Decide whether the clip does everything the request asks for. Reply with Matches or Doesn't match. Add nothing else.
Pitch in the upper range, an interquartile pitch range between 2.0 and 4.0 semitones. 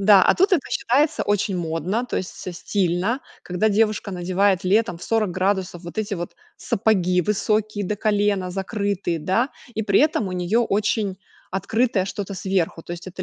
Matches